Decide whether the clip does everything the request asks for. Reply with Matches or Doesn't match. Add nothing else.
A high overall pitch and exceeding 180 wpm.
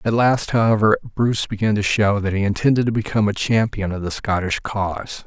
Doesn't match